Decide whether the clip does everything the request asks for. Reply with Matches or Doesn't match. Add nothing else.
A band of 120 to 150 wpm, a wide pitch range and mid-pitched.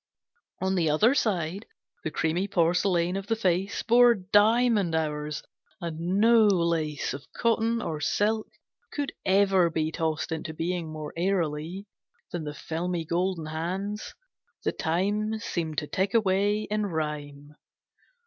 Doesn't match